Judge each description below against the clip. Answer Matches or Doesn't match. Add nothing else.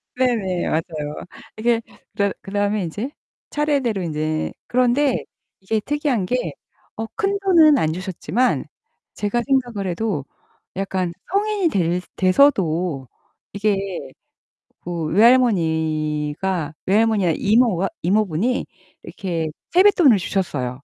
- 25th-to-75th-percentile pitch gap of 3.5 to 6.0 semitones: Doesn't match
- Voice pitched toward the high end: Matches